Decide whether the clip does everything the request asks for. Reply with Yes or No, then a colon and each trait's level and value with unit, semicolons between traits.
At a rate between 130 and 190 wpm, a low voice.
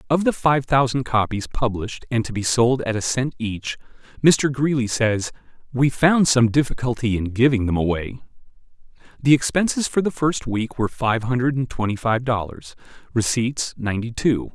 Yes: average, 170 wpm; low, 125 Hz